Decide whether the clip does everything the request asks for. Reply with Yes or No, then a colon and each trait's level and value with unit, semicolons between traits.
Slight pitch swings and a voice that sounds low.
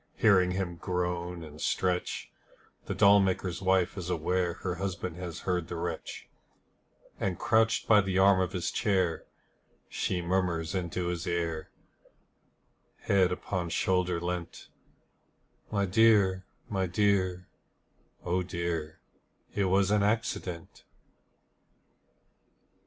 Yes: narrow, 1.8 semitones; very low, 90 Hz